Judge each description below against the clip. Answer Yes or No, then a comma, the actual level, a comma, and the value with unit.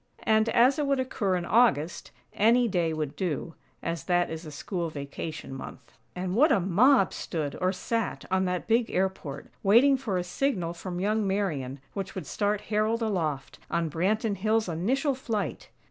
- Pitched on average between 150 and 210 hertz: Yes, high, 190 Hz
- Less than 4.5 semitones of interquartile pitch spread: No, average, 5.0 semitones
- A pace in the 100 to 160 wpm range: No, average, 175 wpm